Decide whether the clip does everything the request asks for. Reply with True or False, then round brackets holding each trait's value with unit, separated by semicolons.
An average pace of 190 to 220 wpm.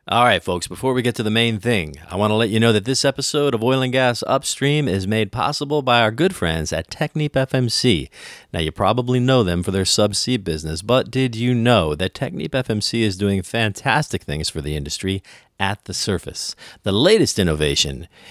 True (205 wpm)